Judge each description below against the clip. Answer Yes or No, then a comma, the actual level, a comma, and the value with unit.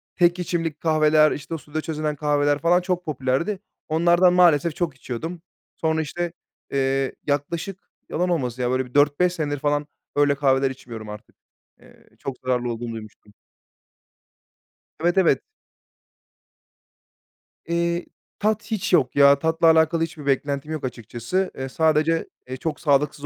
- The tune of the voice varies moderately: Yes, average, 3.8 semitones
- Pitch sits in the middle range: Yes, medium, 150 Hz